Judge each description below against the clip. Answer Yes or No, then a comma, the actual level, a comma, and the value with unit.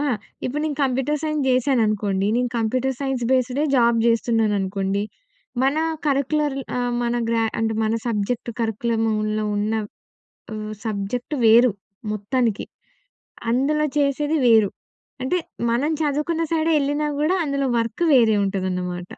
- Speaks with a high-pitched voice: Yes, high, 240 Hz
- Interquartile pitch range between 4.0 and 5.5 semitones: Yes, average, 4.5 semitones